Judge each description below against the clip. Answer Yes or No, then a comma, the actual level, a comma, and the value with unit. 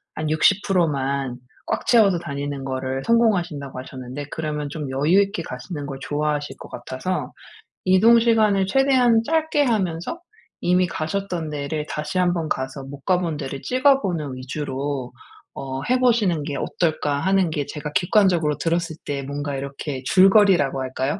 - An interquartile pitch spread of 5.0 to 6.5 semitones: Yes, wide, 5.5 semitones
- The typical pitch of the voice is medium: Yes, medium, 155 Hz